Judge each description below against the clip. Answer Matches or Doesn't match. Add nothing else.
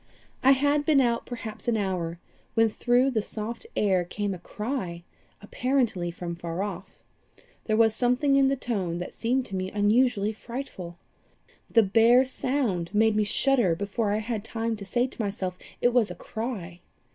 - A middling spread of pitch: Matches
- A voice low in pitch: Doesn't match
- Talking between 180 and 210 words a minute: Doesn't match